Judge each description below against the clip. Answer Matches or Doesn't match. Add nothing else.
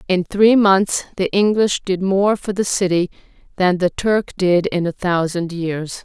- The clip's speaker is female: Matches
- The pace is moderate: Matches